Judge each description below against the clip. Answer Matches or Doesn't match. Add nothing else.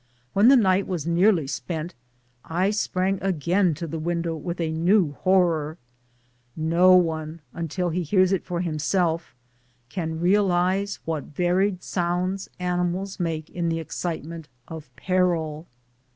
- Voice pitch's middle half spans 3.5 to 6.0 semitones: Doesn't match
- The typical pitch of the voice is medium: Matches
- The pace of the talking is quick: Doesn't match